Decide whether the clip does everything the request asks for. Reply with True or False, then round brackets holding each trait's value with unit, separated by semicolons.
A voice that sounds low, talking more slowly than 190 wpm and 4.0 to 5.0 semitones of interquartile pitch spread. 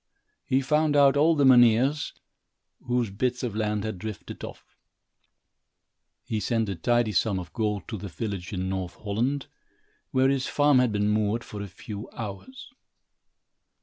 True (110 Hz; 155 wpm; 4.3 semitones)